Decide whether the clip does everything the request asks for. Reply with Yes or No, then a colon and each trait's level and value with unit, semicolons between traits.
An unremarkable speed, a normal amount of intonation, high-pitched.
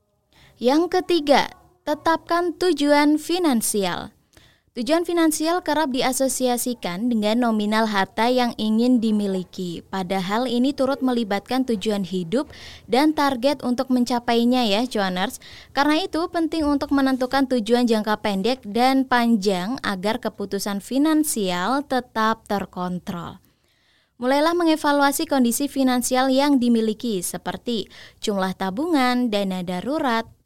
Yes: average, 105 wpm; average, 4.8 semitones; high, 245 Hz